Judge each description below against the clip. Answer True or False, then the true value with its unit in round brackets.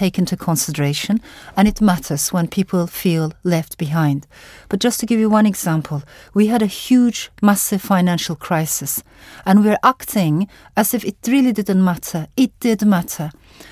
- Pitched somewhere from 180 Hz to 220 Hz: True (190 Hz)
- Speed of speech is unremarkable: True (160 wpm)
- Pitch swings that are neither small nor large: True (4.8 semitones)